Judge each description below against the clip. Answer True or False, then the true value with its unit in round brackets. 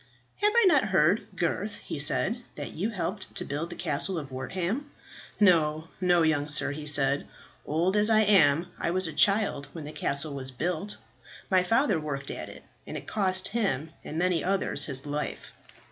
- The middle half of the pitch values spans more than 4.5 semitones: True (5.0 semitones)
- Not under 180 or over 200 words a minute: True (185 wpm)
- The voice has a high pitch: False (170 Hz)